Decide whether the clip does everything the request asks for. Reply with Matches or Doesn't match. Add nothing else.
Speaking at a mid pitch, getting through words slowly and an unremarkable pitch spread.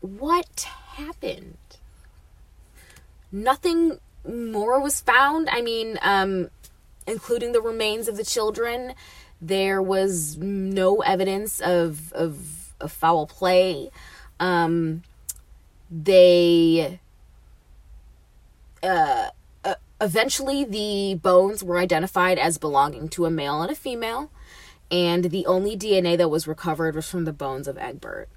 Doesn't match